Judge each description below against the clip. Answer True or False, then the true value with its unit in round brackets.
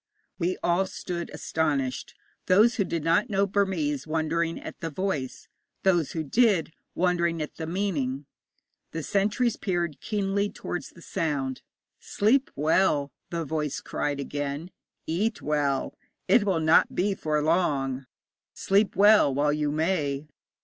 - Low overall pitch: False (165 Hz)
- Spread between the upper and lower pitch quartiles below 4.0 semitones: False (4.6 semitones)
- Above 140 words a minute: False (135 wpm)